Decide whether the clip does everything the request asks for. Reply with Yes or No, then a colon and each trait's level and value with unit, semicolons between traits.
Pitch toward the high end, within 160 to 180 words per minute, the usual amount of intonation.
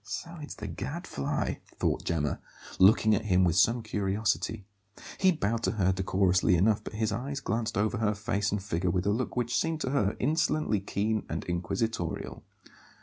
No: low, 105 Hz; average, 175 wpm; average, 3.9 semitones